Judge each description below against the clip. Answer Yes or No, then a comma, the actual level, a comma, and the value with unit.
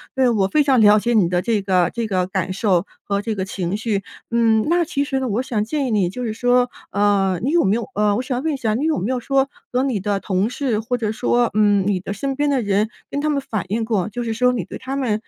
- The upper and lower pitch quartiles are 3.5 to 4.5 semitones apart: Yes, average, 4.0 semitones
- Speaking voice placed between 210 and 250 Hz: Yes, high, 225 Hz